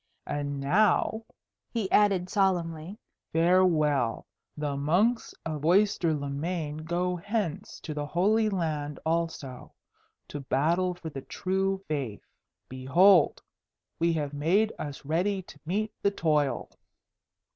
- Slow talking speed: Yes, slow, 120 wpm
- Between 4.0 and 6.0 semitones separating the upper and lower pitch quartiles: Yes, average, 4.5 semitones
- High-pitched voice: No, medium, 165 Hz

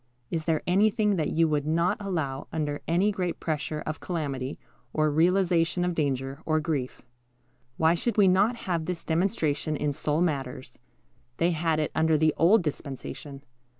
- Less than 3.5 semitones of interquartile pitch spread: Yes, average, 3.0 semitones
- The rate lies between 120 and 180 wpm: Yes, average, 160 wpm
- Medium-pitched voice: Yes, medium, 160 Hz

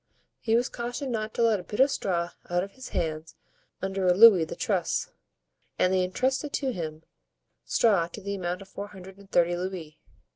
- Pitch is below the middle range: No, high, 190 Hz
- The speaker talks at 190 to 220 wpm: Yes, average, 195 wpm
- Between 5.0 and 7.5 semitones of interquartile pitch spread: No, average, 4.2 semitones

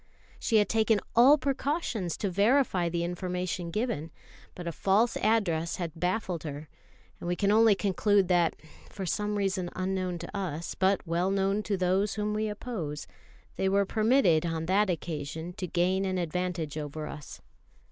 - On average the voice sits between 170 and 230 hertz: Yes, medium, 185 Hz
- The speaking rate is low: No, average, 165 wpm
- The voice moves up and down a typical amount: Yes, average, 3.4 semitones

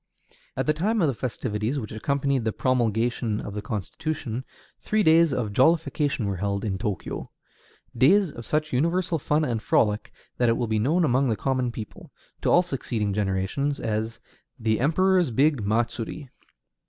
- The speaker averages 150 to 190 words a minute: Yes, average, 165 wpm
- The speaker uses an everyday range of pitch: No, wide, 5.7 semitones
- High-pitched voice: No, low, 125 Hz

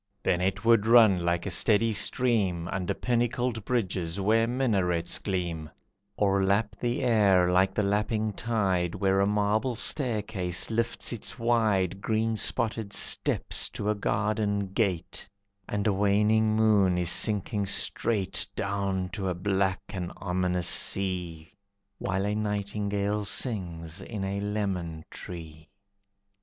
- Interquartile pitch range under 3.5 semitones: Yes, average, 2.9 semitones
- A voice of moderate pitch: No, low, 100 Hz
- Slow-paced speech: Yes, slow, 130 wpm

